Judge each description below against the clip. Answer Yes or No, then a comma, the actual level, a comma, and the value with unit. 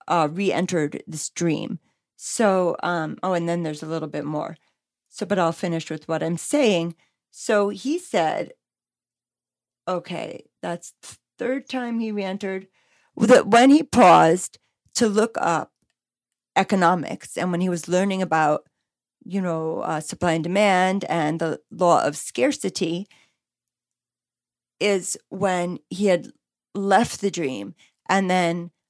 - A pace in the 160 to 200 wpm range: No, average, 140 wpm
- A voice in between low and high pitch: Yes, medium, 175 Hz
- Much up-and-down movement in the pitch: No, average, 3.7 semitones